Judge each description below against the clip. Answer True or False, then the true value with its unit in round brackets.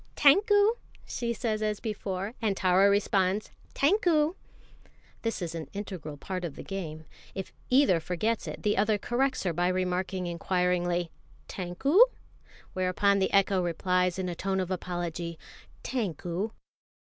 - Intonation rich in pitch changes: False (3.3 semitones)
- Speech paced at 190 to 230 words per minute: False (135 wpm)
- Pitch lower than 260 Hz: True (190 Hz)